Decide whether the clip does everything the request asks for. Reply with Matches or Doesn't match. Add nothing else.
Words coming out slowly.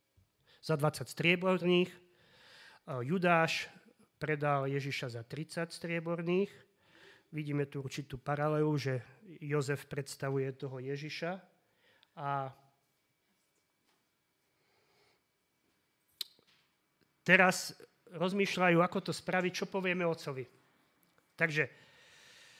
Matches